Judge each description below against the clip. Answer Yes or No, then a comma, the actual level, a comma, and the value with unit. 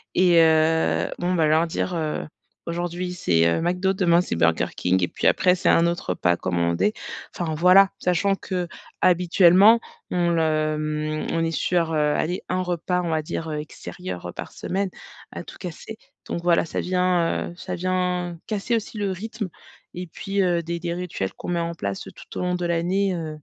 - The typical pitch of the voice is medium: Yes, medium, 175 Hz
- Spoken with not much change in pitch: Yes, narrow, 2.3 semitones